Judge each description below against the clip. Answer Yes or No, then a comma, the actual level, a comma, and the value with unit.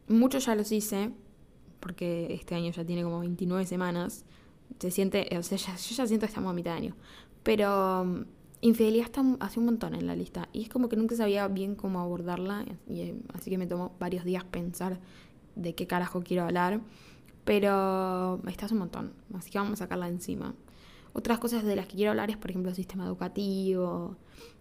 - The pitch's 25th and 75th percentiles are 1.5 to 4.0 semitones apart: Yes, average, 3.1 semitones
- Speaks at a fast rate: Yes, fast, 195 wpm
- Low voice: No, high, 190 Hz